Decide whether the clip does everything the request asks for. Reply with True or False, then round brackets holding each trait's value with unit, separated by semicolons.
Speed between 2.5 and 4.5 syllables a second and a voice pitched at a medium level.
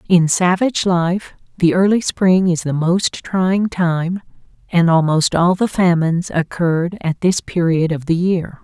True (4.2 syllables/s; 175 Hz)